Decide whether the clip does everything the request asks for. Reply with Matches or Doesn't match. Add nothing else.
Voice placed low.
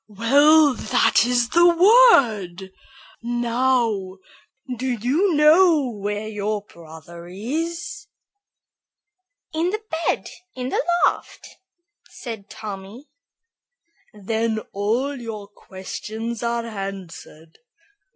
Doesn't match